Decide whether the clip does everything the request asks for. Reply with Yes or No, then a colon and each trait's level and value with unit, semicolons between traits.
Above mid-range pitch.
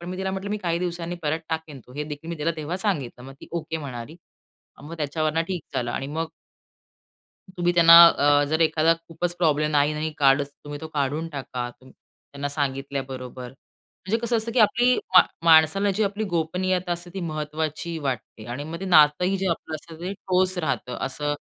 No: medium, 160 Hz